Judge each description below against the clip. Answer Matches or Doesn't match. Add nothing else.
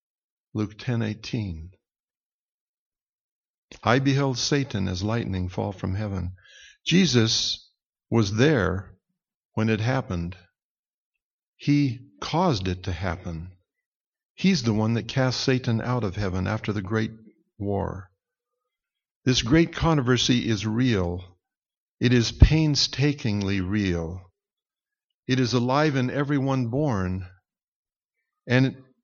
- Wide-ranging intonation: Matches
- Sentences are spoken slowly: Matches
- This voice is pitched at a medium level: Doesn't match